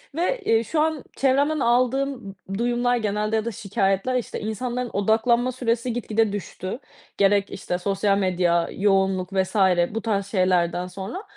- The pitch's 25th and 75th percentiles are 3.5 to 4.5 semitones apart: Yes, average, 4.0 semitones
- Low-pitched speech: No, high, 215 Hz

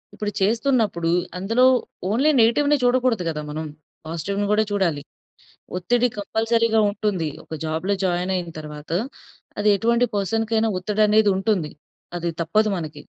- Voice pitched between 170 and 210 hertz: Yes, high, 205 Hz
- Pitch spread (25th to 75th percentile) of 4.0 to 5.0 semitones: Yes, average, 4.7 semitones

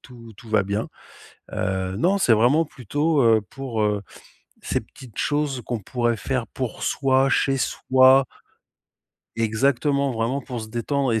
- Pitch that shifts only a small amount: No, average, 3.5 semitones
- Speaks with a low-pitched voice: Yes, low, 125 Hz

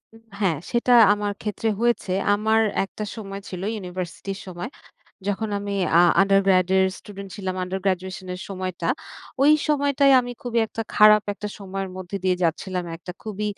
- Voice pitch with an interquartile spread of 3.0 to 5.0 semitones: No, narrow, 2.4 semitones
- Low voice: No, high, 195 Hz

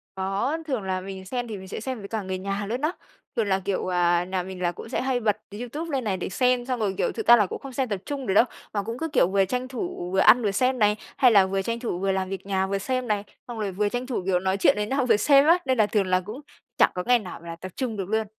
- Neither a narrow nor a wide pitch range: Yes, average, 4.6 semitones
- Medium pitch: No, high, 210 Hz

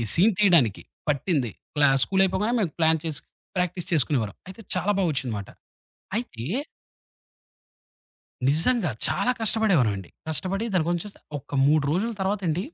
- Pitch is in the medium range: Yes, medium, 170 Hz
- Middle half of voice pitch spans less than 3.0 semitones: No, wide, 5.4 semitones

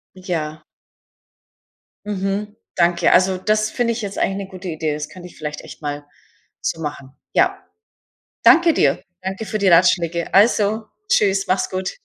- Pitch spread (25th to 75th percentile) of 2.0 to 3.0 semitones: No, average, 4.0 semitones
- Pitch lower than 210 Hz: Yes, medium, 185 Hz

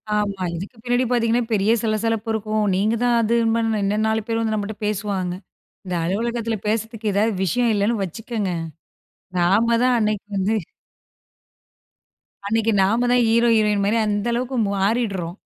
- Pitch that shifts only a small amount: Yes, narrow, 2.3 semitones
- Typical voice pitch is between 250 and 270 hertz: No, high, 220 Hz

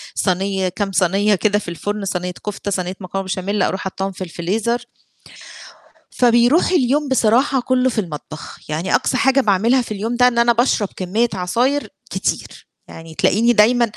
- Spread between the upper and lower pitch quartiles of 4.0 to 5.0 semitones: Yes, average, 4.4 semitones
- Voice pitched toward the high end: Yes, high, 210 Hz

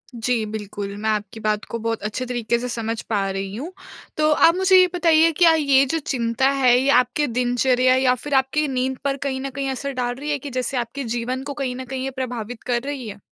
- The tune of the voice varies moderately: Yes, average, 3.1 semitones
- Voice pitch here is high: Yes, very high, 255 Hz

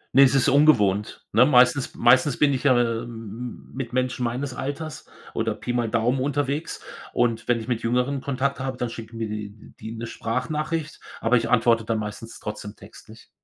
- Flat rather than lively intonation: No, average, 3.0 semitones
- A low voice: Yes, low, 125 Hz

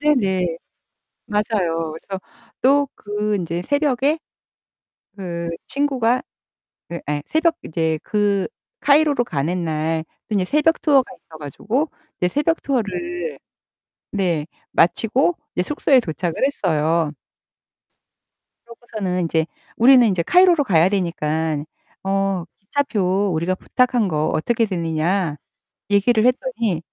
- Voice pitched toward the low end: No, high, 200 Hz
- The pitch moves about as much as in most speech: No, wide, 7.4 semitones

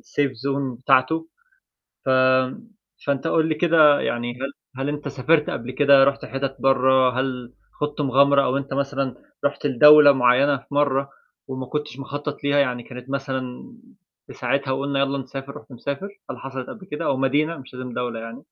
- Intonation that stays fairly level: Yes, narrow, 1.8 semitones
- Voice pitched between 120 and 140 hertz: Yes, low, 135 Hz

